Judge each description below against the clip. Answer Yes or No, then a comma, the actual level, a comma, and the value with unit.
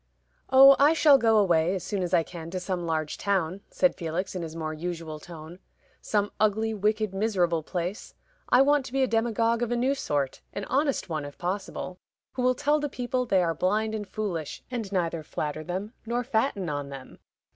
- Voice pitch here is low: No, high, 195 Hz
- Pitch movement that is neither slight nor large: No, wide, 5.8 semitones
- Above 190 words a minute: Yes, average, 200 wpm